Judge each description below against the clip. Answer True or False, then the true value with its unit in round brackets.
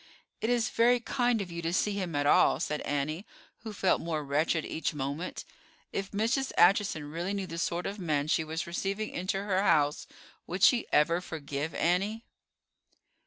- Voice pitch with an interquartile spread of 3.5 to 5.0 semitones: True (4.5 semitones)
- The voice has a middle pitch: True (175 Hz)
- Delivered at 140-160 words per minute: False (175 wpm)